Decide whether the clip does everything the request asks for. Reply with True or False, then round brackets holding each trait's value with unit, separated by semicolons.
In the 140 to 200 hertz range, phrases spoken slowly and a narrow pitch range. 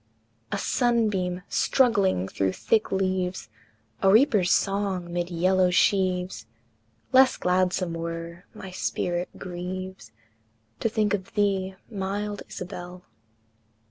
True (185 Hz; 105 wpm; 2.2 semitones)